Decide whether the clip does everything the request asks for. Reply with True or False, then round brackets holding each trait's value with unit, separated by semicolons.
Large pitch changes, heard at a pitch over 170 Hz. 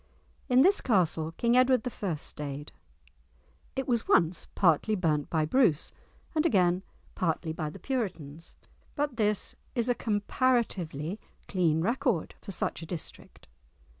True (7.2 semitones; 190 Hz)